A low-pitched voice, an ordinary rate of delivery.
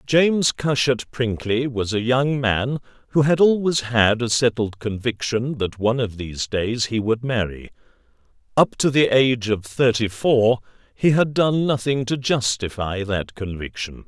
Yes: low, 120 Hz; average, 160 wpm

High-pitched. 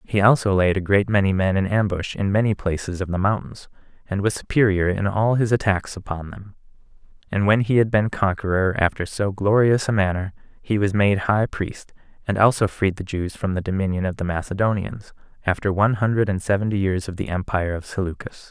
No: low, 100 Hz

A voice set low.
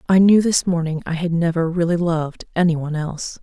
No: medium, 170 Hz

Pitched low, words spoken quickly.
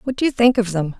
No: high, 220 Hz; fast, 365 wpm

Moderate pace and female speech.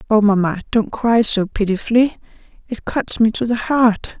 Yes: average, 155 wpm; female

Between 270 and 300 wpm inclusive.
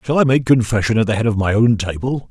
Yes: fast, 285 wpm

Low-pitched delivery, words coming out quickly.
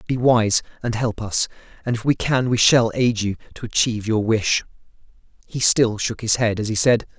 Yes: low, 115 Hz; fast, 210 wpm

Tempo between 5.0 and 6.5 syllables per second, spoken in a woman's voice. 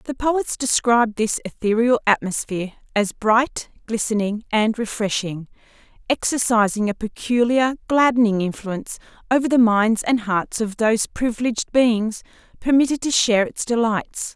No: 4.8 syllables/s; female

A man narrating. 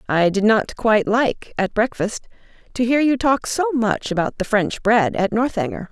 No: female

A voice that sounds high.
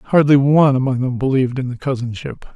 No: low, 135 Hz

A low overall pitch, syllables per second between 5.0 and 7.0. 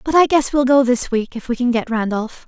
No: very high, 250 Hz; 5.5 syllables/s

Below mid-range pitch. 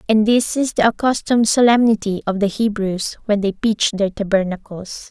No: high, 210 Hz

